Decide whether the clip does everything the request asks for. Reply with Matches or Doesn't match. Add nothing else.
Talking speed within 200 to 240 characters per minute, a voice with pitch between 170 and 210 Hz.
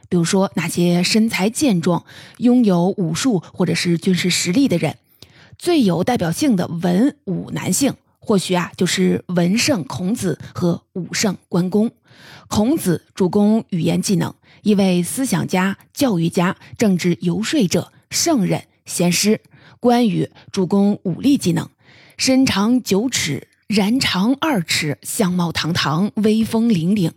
Matches